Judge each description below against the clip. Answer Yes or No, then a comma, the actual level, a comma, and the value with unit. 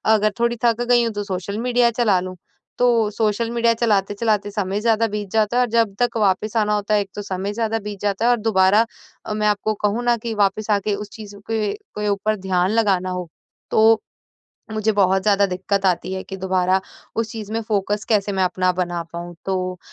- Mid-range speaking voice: No, high, 210 Hz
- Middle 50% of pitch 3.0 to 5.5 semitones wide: No, narrow, 2.6 semitones